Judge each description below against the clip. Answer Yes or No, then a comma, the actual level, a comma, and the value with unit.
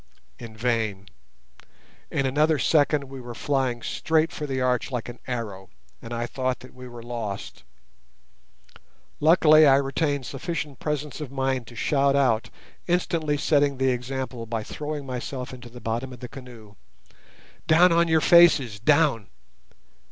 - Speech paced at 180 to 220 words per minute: No, average, 145 wpm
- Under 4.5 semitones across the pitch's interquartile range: Yes, average, 3.6 semitones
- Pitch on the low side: Yes, low, 130 Hz